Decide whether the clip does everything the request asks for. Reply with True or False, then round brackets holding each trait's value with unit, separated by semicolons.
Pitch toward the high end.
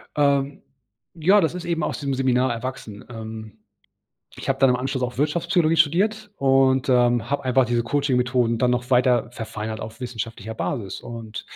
False (130 Hz)